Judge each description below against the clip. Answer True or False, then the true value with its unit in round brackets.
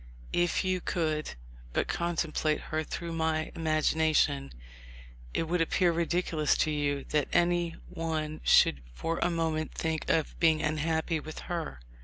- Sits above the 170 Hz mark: False (160 Hz)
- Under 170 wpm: True (140 wpm)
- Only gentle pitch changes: True (1.5 semitones)